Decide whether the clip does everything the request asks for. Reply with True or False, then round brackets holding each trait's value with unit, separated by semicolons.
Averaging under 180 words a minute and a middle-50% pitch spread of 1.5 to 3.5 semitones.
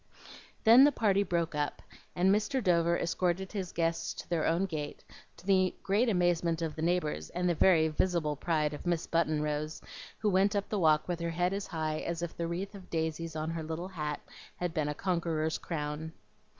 False (205 wpm; 2.8 semitones)